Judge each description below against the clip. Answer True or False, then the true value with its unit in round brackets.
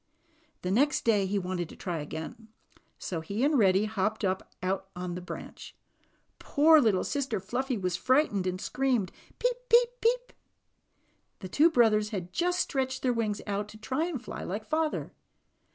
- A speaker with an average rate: True (175 wpm)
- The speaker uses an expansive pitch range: True (6.9 semitones)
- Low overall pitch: False (215 Hz)